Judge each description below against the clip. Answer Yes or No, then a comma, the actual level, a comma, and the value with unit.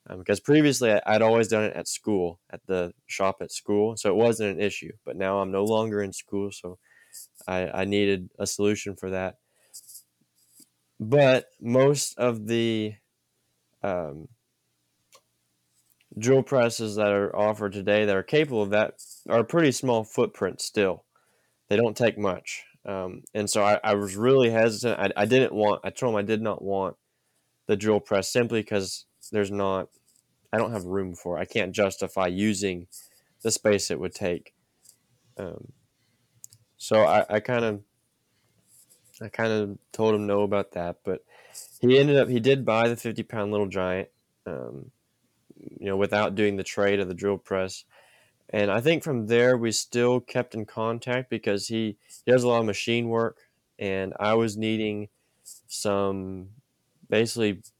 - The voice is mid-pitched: No, low, 105 Hz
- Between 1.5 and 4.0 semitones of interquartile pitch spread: Yes, average, 2.9 semitones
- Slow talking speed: No, average, 165 wpm